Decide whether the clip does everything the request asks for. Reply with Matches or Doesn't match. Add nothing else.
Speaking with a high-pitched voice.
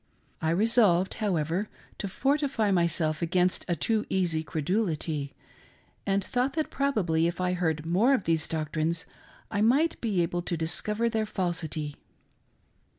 Doesn't match